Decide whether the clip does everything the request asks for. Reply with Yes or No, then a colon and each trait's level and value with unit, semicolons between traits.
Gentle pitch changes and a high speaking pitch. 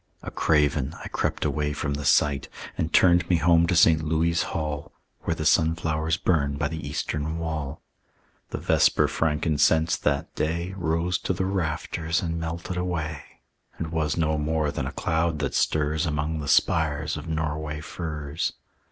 No: narrow, 1.7 semitones; very low, 80 Hz